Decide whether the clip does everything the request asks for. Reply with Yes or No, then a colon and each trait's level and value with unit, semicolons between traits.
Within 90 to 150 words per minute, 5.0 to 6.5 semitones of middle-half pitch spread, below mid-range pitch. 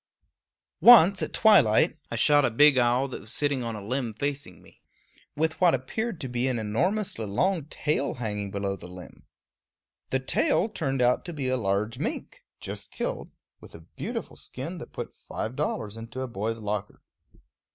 No: average, 175 wpm; wide, 5.4 semitones; low, 125 Hz